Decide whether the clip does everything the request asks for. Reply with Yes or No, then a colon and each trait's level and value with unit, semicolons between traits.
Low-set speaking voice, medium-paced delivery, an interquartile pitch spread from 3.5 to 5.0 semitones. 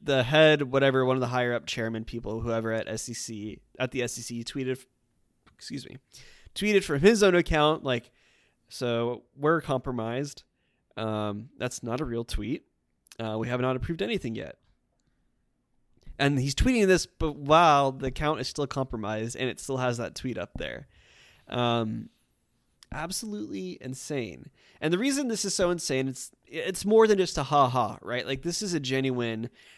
Yes: low, 130 Hz; average, 170 wpm; average, 4.5 semitones